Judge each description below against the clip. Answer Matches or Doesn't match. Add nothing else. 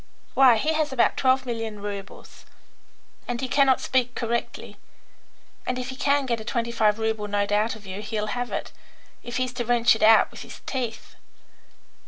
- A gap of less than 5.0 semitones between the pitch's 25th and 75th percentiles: Matches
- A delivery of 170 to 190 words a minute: Matches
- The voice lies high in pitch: Matches